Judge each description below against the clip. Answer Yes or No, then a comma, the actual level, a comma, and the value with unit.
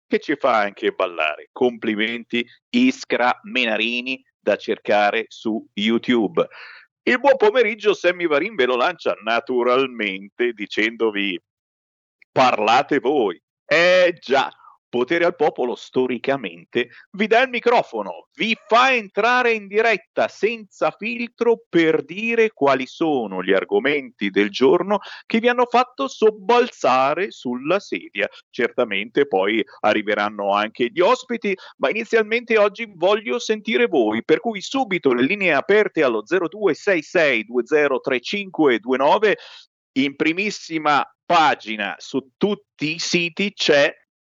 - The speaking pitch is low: No, medium, 175 Hz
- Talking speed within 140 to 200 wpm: No, slow, 115 wpm